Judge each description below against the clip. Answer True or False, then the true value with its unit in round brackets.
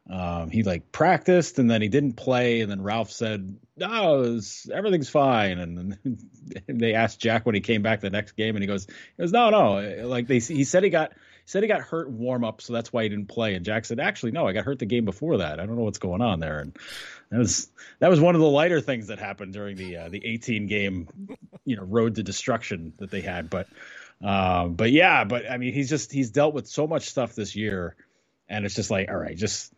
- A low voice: True (115 Hz)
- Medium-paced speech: False (250 wpm)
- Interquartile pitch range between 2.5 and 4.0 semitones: False (4.8 semitones)